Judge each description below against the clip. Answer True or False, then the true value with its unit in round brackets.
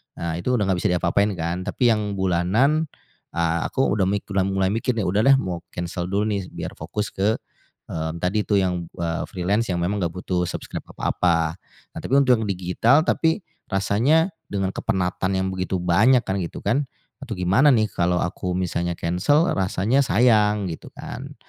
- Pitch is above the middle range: False (95 Hz)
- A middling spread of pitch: True (3.8 semitones)